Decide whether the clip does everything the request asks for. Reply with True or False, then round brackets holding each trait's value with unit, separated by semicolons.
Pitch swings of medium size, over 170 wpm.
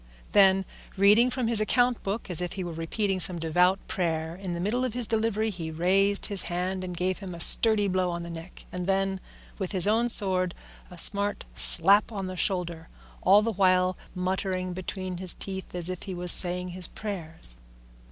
False (2.3 semitones; 195 wpm)